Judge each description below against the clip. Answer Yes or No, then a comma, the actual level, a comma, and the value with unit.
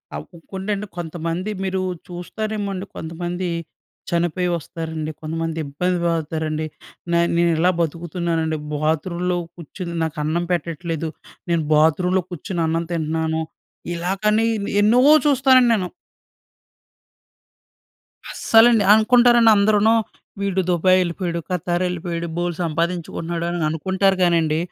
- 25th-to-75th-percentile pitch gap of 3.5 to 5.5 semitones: No, average, 2.7 semitones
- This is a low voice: No, medium, 175 Hz